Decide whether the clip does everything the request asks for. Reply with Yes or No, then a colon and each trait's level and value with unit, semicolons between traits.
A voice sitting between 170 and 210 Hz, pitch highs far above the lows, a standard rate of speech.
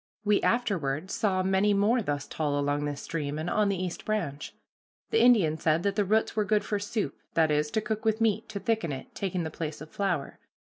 No: high, 190 Hz; wide, 5.7 semitones; fast, 220 wpm